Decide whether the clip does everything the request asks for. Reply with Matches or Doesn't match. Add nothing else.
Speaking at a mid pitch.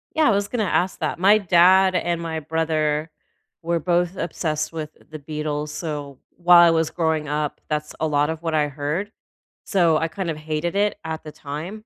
Matches